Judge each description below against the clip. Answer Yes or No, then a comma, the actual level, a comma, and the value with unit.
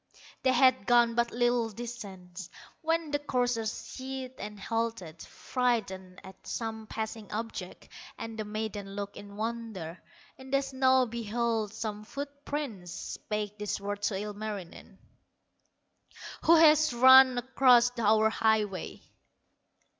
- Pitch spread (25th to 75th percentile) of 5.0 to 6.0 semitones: No, average, 3.5 semitones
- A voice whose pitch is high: Yes, high, 225 Hz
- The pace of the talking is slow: Yes, slow, 125 wpm